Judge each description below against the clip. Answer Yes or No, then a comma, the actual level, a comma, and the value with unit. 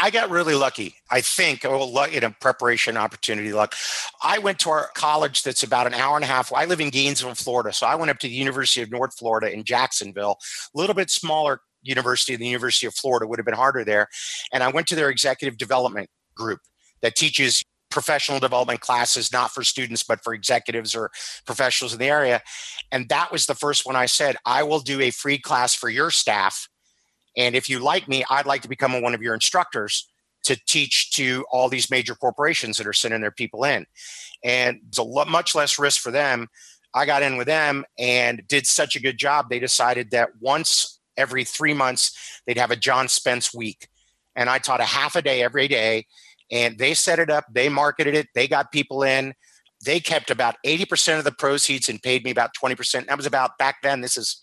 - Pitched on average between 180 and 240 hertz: No, low, 130 Hz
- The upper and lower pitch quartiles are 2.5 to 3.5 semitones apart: Yes, average, 2.9 semitones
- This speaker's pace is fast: Yes, fast, 220 wpm